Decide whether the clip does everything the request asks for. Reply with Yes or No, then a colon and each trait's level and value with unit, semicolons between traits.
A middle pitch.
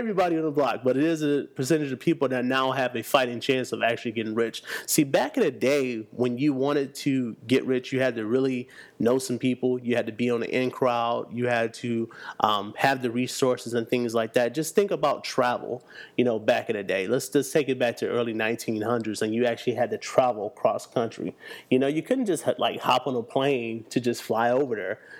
No: low, 125 Hz